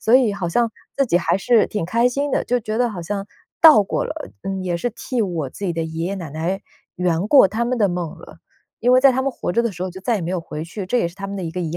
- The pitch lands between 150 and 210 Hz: Yes, high, 195 Hz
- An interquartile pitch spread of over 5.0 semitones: Yes, wide, 5.4 semitones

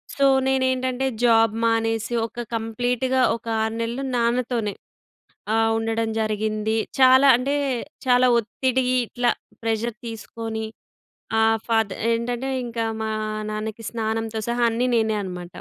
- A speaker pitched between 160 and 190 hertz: No, high, 230 Hz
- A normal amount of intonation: No, narrow, 1.9 semitones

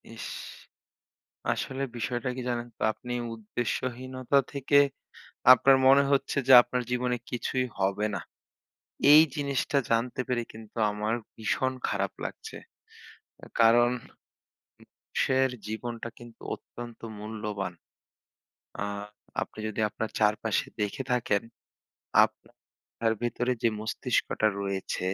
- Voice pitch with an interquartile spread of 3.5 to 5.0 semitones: No, average, 3.0 semitones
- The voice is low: Yes, low, 120 Hz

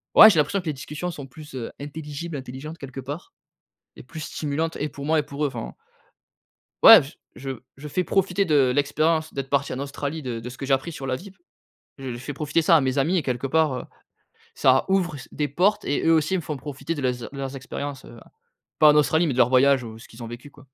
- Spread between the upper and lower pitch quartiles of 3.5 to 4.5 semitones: No, average, 3.1 semitones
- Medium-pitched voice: Yes, medium, 145 Hz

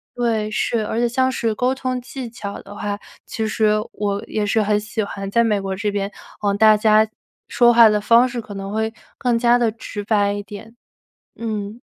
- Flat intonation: Yes, narrow, 2.3 semitones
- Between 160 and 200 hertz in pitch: No, high, 215 Hz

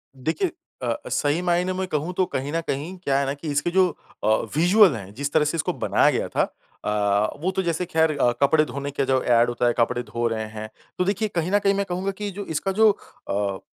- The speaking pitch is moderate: Yes, medium, 155 Hz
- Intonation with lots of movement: Yes, wide, 6.9 semitones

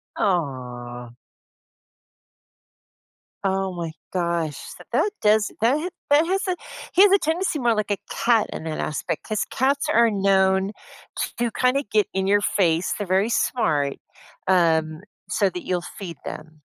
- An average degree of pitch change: No, wide, 5.9 semitones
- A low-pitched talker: No, high, 195 Hz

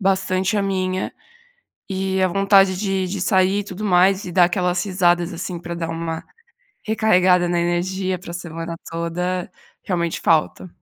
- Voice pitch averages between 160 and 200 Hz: Yes, medium, 185 Hz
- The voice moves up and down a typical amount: No, narrow, 1.7 semitones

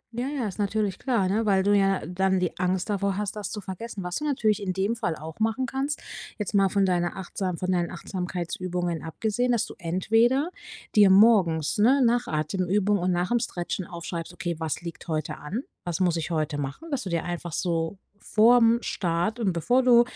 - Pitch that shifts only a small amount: No, average, 4.3 semitones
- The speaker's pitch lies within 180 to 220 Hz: Yes, high, 190 Hz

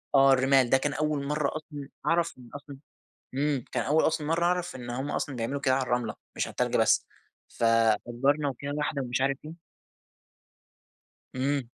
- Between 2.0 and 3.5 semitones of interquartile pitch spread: Yes, narrow, 2.6 semitones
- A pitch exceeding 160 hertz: No, medium, 140 Hz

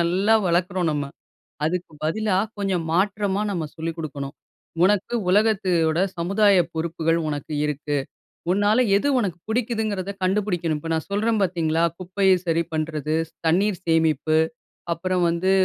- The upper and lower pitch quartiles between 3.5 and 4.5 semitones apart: Yes, average, 3.8 semitones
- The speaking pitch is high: No, medium, 180 Hz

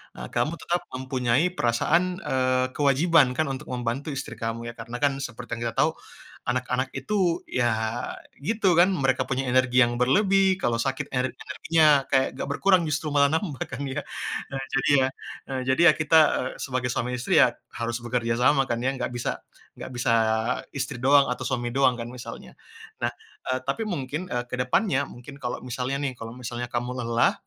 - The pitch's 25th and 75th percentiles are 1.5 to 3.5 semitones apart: Yes, average, 2.7 semitones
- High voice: No, low, 130 Hz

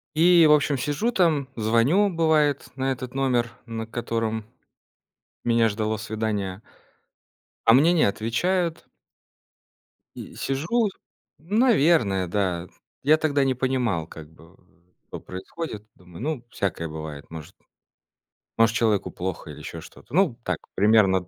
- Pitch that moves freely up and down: Yes, wide, 7.0 semitones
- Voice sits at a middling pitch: No, low, 115 Hz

